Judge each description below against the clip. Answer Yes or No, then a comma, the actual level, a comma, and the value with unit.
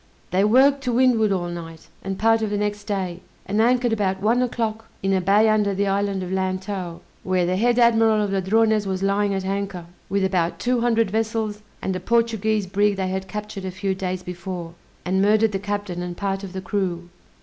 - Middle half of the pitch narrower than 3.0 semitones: Yes, narrow, 2.6 semitones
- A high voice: Yes, high, 200 Hz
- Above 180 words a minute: Yes, fast, 205 wpm